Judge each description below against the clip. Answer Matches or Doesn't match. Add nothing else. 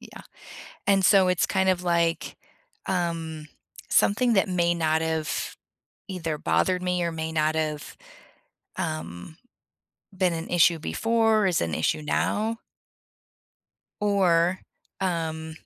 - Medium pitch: Matches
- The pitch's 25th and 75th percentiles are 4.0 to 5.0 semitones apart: Doesn't match